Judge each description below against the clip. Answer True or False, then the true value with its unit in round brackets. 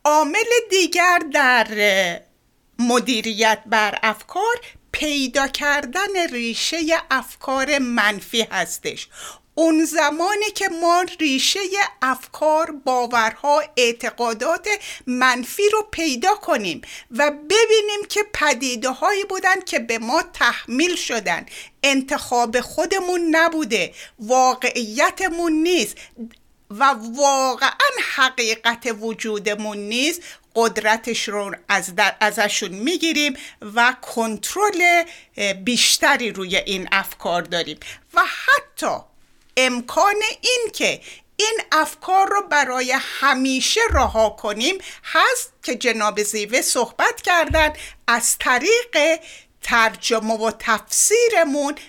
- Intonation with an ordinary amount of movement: False (6.9 semitones)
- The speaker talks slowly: True (95 wpm)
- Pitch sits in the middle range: False (275 Hz)